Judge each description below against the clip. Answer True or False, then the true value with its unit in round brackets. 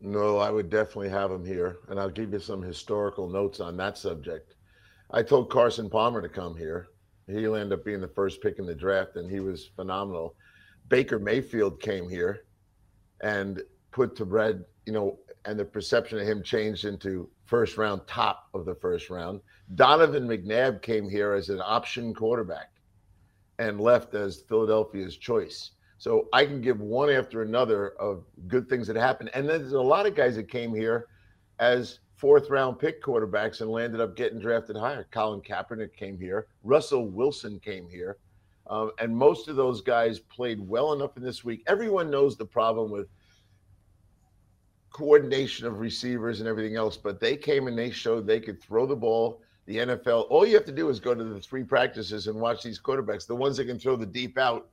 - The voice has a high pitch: False (110 Hz)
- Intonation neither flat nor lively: True (3.6 semitones)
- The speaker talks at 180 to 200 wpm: True (190 wpm)